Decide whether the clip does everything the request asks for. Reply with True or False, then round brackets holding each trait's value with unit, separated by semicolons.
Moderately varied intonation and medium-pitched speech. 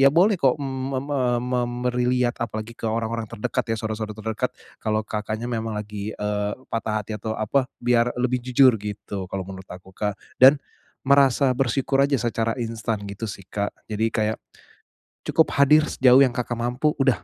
False (3.1 semitones; 115 Hz)